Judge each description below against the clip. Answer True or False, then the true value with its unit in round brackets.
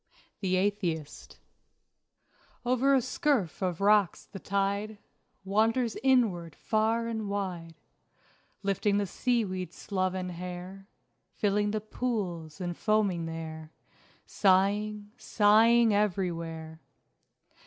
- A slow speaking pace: True (100 wpm)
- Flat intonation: False (3.3 semitones)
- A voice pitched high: True (200 Hz)